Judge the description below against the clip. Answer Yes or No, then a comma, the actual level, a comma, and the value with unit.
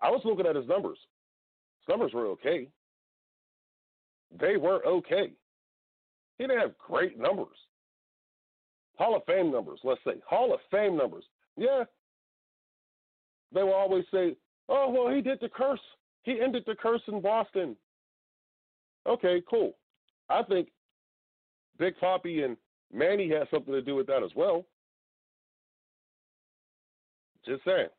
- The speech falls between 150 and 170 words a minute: No, slow, 135 wpm